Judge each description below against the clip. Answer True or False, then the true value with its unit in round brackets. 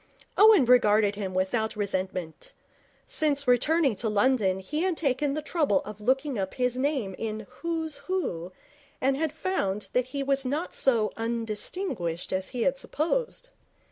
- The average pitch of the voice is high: True (255 Hz)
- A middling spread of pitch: False (6.3 semitones)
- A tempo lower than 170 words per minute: True (150 wpm)